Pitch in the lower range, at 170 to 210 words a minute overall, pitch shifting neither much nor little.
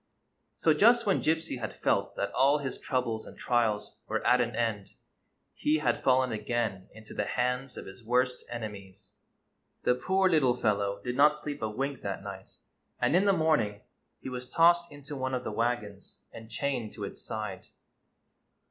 Yes: low, 125 Hz; average, 175 wpm; average, 4.9 semitones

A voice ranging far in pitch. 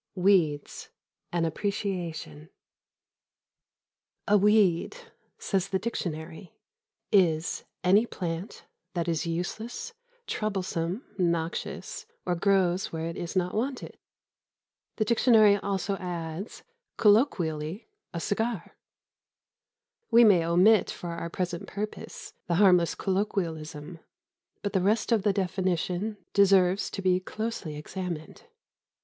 No: average, 3.4 semitones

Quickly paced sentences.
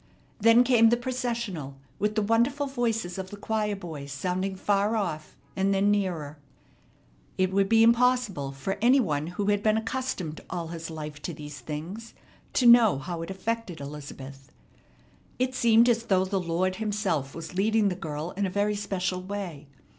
No: average, 170 wpm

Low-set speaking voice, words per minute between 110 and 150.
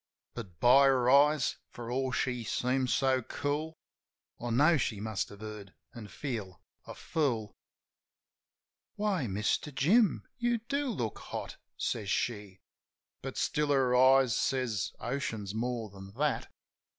Yes: low, 125 Hz; slow, 135 wpm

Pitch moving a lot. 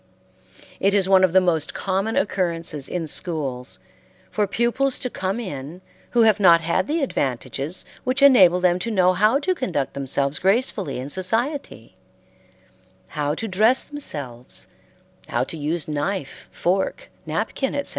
Yes: wide, 6.4 semitones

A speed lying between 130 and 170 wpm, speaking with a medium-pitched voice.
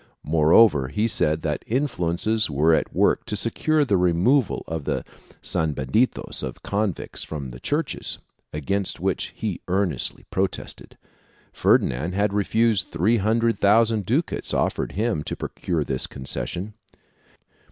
No: slow, 135 wpm; very low, 95 Hz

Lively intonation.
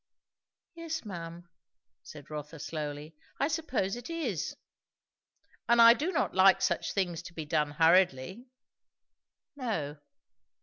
Yes: wide, 7.9 semitones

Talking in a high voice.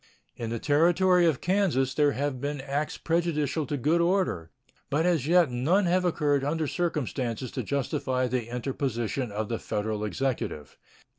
No: medium, 140 Hz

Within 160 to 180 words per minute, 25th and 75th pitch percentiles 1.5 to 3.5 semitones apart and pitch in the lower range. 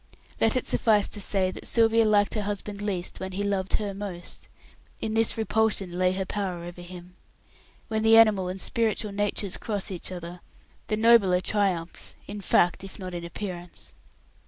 No: average, 175 wpm; average, 2.8 semitones; high, 200 Hz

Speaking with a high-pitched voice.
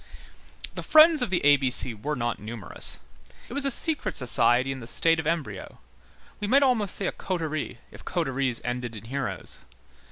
No: medium, 145 Hz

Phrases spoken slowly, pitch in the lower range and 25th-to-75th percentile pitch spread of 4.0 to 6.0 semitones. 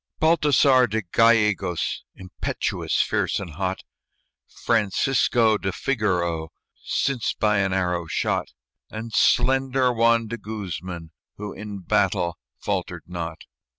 Yes: slow, 110 wpm; low, 105 Hz; average, 4.6 semitones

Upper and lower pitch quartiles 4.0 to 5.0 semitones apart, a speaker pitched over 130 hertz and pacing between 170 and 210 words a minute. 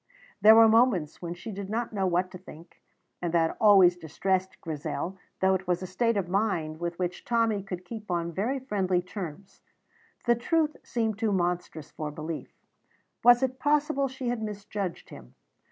Yes: average, 4.5 semitones; high, 190 Hz; average, 175 wpm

